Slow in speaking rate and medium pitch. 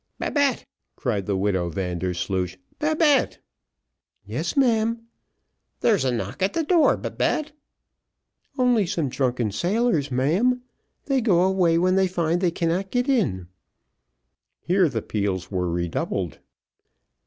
Yes: slow, 120 wpm; medium, 175 Hz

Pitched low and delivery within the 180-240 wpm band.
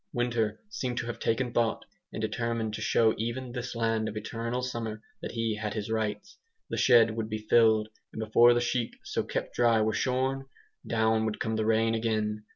Yes: low, 115 Hz; average, 195 wpm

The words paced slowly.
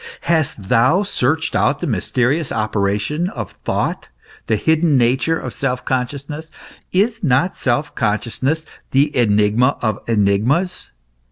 Yes: slow, 120 wpm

